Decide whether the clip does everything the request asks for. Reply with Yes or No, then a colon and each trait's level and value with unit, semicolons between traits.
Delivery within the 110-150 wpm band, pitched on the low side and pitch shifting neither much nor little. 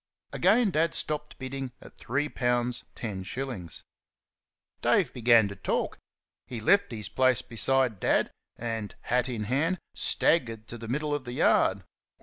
Yes: average, 145 wpm; low, 125 Hz; average, 4.0 semitones